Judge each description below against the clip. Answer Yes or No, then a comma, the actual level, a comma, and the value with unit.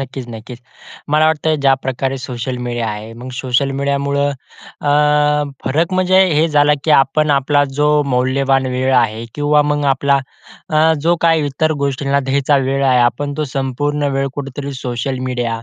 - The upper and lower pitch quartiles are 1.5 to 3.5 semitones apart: Yes, narrow, 2.5 semitones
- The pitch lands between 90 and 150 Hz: Yes, low, 135 Hz